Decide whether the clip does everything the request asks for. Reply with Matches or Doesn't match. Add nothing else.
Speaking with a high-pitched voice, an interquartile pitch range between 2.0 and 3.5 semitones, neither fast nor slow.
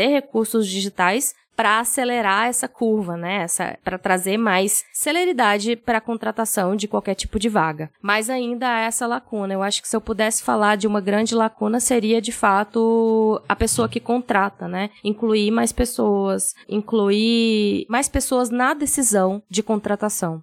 Matches